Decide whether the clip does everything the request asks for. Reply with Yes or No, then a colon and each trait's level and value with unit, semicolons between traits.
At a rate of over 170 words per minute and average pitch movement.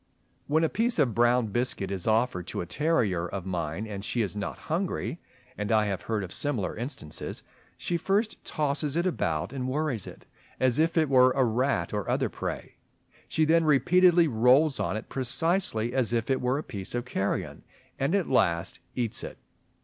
No: average, 190 wpm; wide, 6.7 semitones